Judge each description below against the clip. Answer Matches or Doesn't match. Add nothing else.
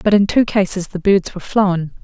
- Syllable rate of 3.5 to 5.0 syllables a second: Doesn't match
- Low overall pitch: Doesn't match